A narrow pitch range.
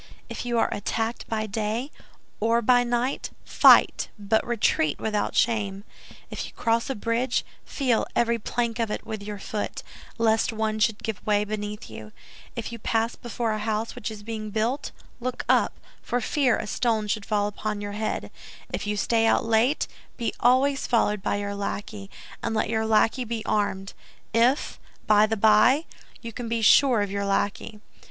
Yes: narrow, 2.1 semitones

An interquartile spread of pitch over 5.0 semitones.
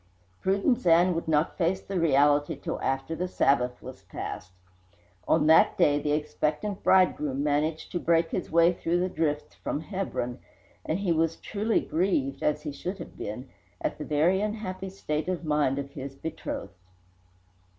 No: average, 4.0 semitones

